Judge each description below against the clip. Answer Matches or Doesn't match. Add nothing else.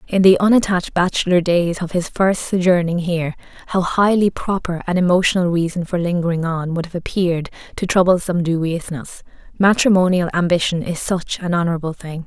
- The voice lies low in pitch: Doesn't match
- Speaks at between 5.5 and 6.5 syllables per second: Matches